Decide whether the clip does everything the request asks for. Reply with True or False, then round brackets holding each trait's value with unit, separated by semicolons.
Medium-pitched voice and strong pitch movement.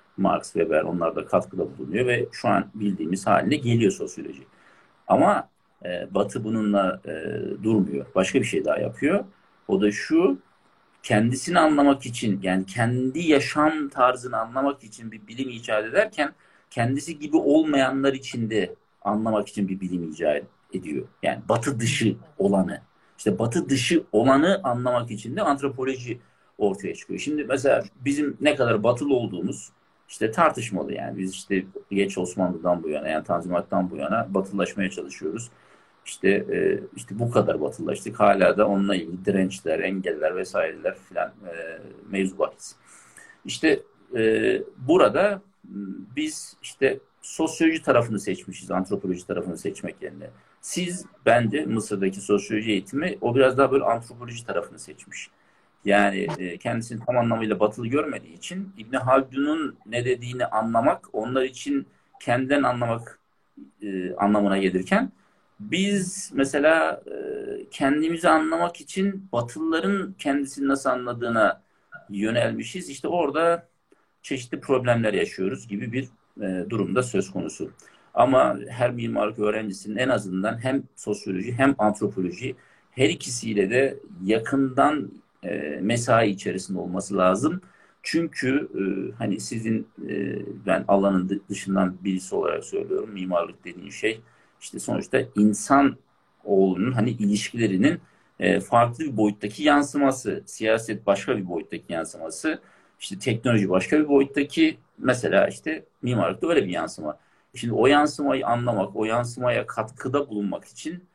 False (120 Hz; 5.8 semitones)